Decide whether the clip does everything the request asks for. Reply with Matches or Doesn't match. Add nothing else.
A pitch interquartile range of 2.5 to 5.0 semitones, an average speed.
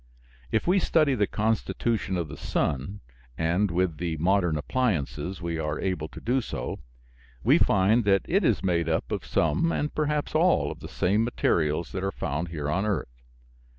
Doesn't match